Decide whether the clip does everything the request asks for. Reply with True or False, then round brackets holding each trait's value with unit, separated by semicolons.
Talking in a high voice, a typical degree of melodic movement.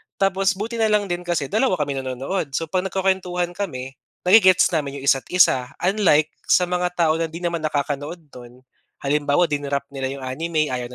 False (165 Hz; 4.7 semitones)